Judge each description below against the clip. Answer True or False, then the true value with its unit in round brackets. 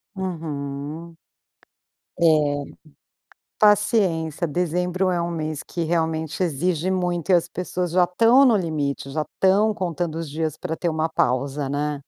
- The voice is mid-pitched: True (170 Hz)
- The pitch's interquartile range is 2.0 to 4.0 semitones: True (2.9 semitones)